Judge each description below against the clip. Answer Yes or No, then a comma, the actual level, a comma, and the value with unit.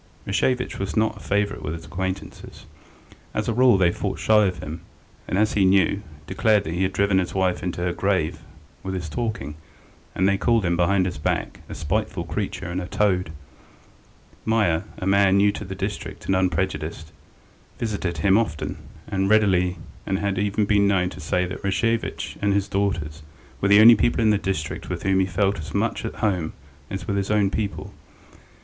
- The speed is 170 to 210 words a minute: Yes, average, 195 wpm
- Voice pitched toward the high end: No, very low, 95 Hz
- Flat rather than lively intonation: Yes, narrow, 2.3 semitones